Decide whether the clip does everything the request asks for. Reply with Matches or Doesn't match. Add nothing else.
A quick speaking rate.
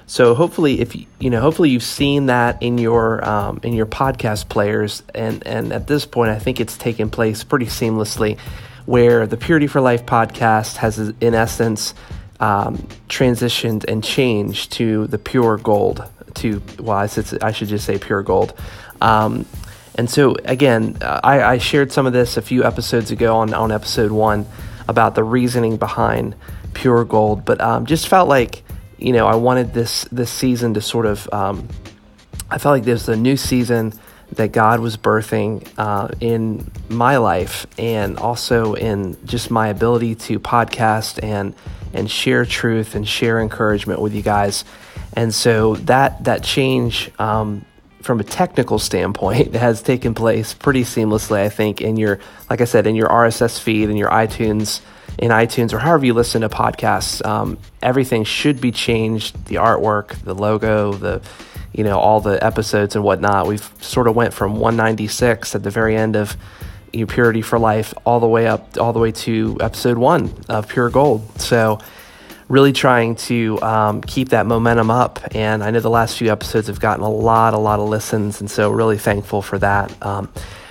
Doesn't match